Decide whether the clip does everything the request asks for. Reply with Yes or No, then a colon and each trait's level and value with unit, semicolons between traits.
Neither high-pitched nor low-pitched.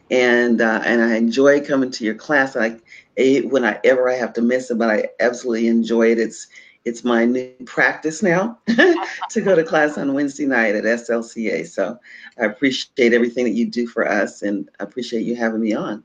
No: low, 120 Hz